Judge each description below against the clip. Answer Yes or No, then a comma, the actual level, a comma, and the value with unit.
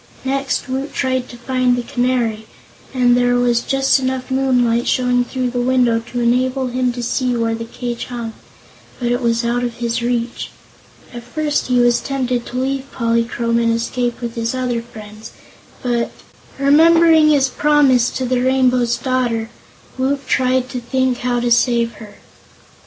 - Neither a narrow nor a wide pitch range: No, narrow, 1.7 semitones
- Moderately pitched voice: No, high, 245 Hz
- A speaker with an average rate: Yes, average, 165 wpm